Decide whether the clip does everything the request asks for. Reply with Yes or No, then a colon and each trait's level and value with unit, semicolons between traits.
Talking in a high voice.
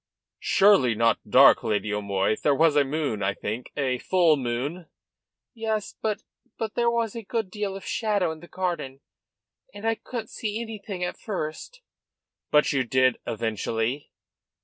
No: medium, 160 Hz